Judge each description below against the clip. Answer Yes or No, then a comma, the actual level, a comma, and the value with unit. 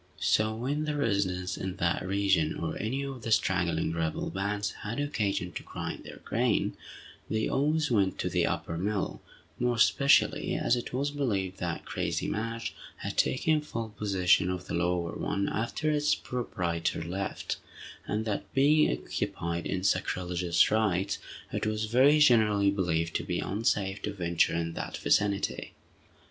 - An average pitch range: Yes, average, 4.7 semitones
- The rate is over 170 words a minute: No, average, 155 wpm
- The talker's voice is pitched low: Yes, low, 100 Hz